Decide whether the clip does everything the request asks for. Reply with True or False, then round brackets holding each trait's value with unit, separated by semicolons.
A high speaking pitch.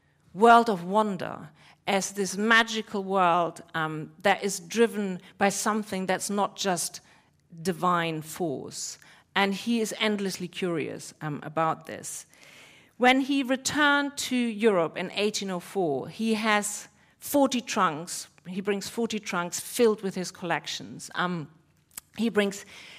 True (195 Hz)